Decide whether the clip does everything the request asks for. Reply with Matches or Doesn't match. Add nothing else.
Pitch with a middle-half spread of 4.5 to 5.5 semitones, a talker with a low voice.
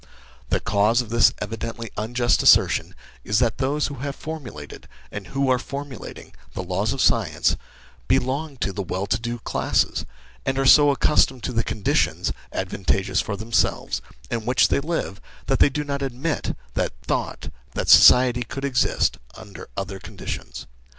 Matches